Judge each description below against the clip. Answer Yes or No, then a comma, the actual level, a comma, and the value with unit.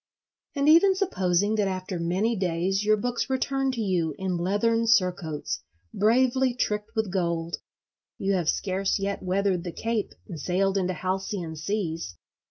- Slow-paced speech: No, average, 150 wpm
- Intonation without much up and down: No, average, 4.0 semitones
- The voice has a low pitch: No, high, 195 Hz